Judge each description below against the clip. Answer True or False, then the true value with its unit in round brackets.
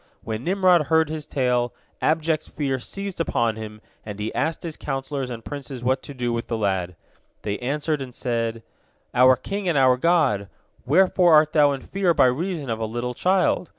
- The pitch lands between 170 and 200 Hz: False (135 Hz)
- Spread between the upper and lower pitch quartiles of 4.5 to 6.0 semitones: True (5.2 semitones)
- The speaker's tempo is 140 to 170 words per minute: False (185 wpm)